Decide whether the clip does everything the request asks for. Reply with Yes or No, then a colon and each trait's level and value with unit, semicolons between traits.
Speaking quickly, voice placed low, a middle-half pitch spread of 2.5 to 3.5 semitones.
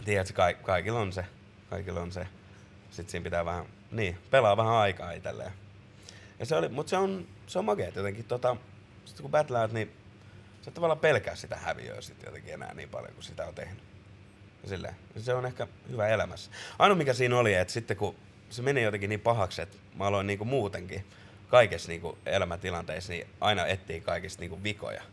Yes: fast, 190 wpm; low, 100 Hz; average, 2.8 semitones